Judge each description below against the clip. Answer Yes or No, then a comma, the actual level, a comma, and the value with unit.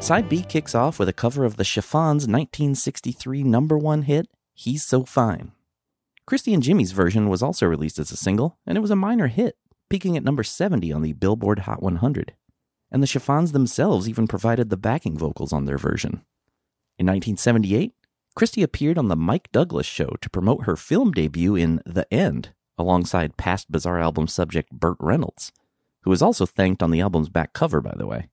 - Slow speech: No, average, 190 wpm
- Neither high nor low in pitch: No, low, 110 Hz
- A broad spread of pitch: Yes, wide, 8.4 semitones